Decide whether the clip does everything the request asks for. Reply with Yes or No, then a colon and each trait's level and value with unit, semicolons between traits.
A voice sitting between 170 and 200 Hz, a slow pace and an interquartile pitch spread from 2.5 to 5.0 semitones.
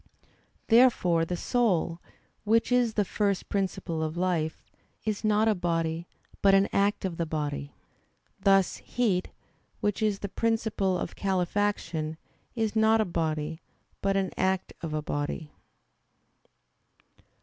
Yes: high, 190 Hz; slow, 130 wpm; average, 4.2 semitones